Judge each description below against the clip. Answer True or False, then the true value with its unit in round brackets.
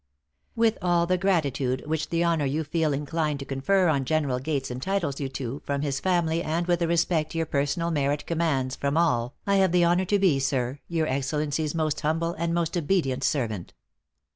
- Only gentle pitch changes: False (3.6 semitones)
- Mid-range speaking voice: True (155 Hz)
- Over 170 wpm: True (190 wpm)